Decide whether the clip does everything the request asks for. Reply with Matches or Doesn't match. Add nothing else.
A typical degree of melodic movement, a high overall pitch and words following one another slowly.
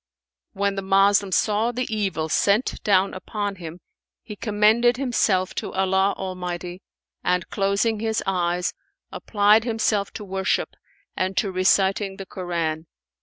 Doesn't match